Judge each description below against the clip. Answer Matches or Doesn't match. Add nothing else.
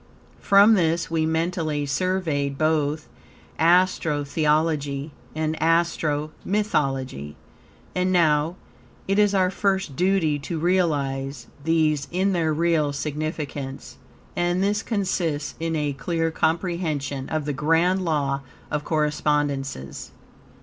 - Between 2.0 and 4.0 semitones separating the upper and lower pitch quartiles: Matches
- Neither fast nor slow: Doesn't match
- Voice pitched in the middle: Matches